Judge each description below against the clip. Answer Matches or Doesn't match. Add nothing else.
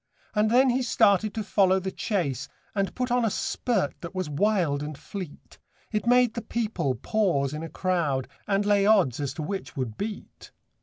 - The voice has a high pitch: Matches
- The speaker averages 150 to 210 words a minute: Matches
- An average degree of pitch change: Doesn't match